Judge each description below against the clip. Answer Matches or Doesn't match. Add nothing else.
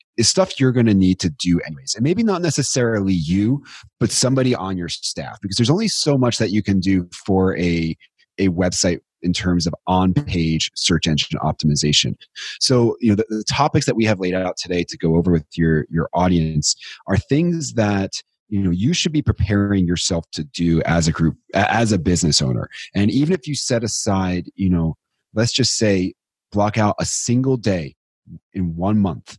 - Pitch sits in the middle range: Doesn't match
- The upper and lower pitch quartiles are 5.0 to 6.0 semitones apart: Matches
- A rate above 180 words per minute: Matches